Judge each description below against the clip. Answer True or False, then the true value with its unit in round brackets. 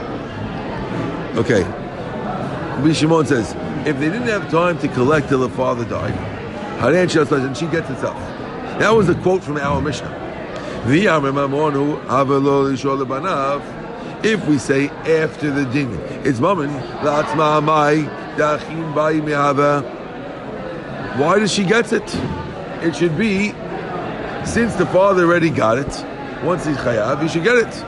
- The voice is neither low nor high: True (150 Hz)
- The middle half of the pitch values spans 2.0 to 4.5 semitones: True (3.7 semitones)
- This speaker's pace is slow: True (120 wpm)